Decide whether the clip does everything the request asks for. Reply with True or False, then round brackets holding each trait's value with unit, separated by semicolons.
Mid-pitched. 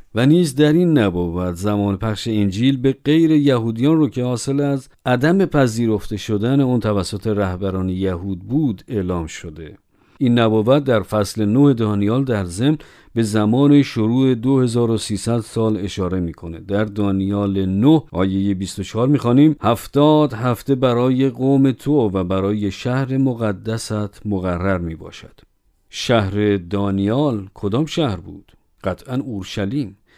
False (110 Hz)